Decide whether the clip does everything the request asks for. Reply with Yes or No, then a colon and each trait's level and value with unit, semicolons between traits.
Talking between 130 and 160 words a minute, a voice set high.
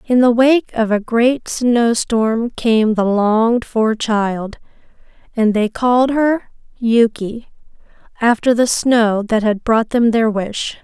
Yes: average, 150 wpm; high, 230 Hz